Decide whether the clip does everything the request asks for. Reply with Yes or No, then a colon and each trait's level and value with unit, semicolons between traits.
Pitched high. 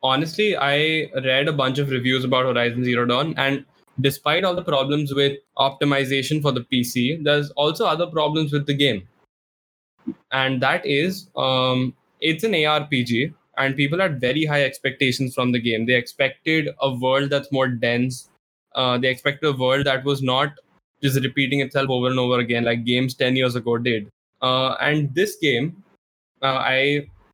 No: low, 135 Hz